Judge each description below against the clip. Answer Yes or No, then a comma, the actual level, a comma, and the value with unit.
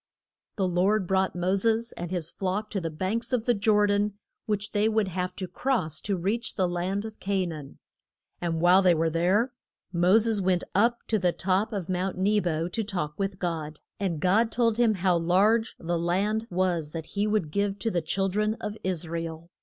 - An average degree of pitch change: Yes, average, 3.4 semitones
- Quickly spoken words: Yes, fast, 210 wpm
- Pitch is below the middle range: No, high, 190 Hz